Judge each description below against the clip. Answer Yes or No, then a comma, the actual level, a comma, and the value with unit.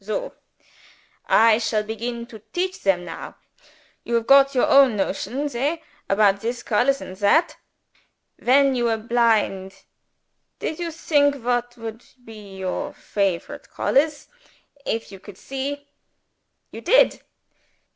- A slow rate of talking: Yes, slow, 130 wpm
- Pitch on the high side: Yes, high, 235 Hz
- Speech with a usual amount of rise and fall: Yes, average, 4.7 semitones